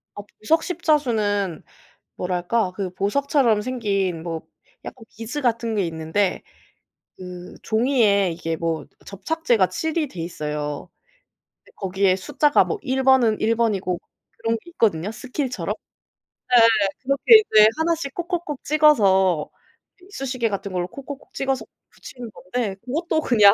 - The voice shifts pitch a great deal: Yes, wide, 6.3 semitones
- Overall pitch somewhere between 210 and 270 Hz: Yes, high, 220 Hz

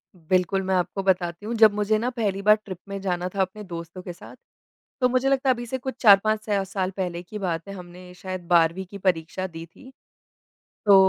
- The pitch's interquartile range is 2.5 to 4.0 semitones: Yes, average, 3.1 semitones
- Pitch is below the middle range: No, high, 190 Hz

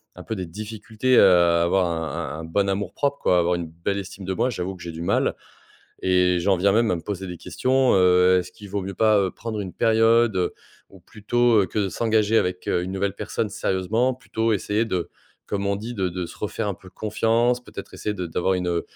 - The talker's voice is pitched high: No, very low, 95 Hz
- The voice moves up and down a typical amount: Yes, average, 3.4 semitones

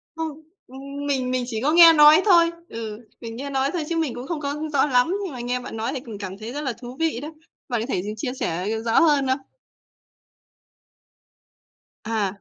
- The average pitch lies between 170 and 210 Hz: No, very high, 260 Hz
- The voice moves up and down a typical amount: Yes, average, 4.5 semitones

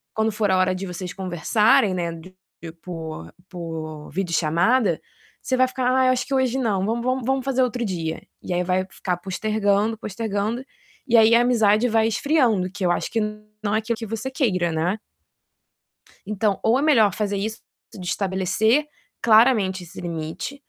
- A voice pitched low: No, high, 210 Hz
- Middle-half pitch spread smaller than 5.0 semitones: Yes, average, 4.3 semitones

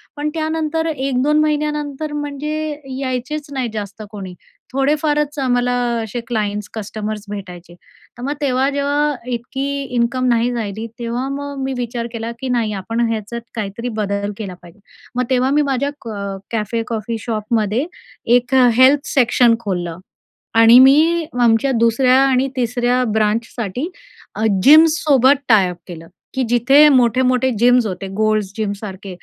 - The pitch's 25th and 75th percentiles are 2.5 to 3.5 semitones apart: No, average, 4.3 semitones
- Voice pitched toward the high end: Yes, high, 245 Hz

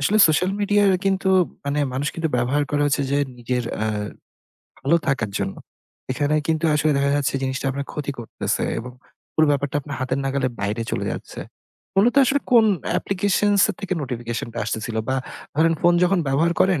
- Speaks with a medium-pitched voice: Yes, medium, 145 Hz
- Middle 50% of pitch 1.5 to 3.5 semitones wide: No, average, 4.5 semitones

